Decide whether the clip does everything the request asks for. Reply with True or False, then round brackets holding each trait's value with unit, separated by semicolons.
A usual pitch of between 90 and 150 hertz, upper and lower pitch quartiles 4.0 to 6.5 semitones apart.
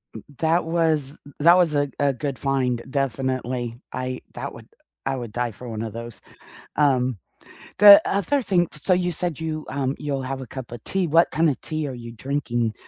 True (135 Hz; 4.4 semitones)